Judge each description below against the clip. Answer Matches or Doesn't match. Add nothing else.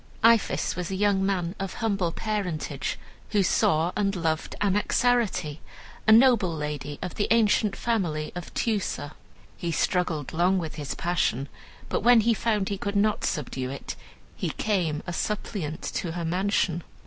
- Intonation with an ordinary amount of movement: Matches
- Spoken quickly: Doesn't match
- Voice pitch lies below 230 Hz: Matches